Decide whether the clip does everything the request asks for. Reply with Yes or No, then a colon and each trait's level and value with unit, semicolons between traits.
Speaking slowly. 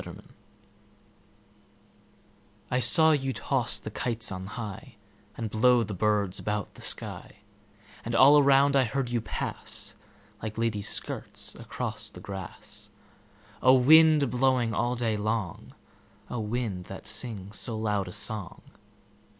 Yes: slow, 125 wpm